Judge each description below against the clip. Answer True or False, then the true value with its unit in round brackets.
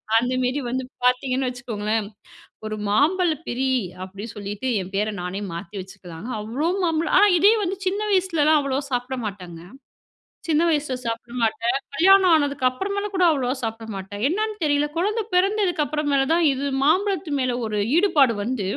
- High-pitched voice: True (265 Hz)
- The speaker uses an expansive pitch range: True (7.3 semitones)